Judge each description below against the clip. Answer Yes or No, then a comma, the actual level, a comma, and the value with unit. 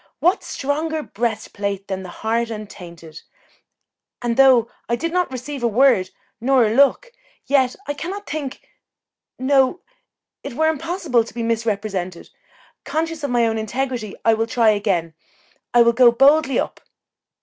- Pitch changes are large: No, average, 4.4 semitones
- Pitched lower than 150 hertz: No, high, 240 Hz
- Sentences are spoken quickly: No, average, 150 wpm